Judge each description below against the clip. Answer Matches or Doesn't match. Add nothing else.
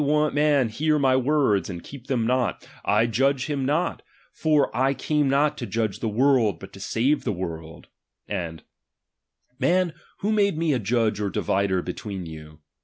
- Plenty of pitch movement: Matches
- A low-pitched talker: Matches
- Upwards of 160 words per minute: Matches